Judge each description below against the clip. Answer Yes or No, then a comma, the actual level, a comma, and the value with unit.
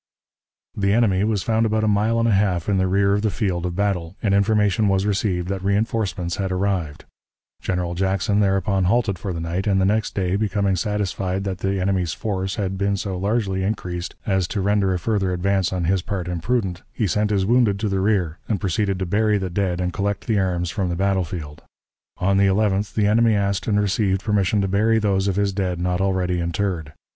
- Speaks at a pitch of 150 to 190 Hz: No, very low, 95 Hz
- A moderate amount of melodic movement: No, narrow, 2.0 semitones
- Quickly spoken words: Yes, fast, 210 wpm